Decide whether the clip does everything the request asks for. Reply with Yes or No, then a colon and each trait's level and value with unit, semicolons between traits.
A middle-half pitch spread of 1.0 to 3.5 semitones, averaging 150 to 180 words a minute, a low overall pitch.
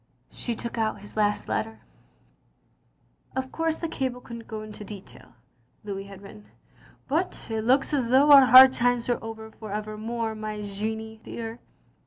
No: average, 2.7 semitones; average, 160 wpm; high, 225 Hz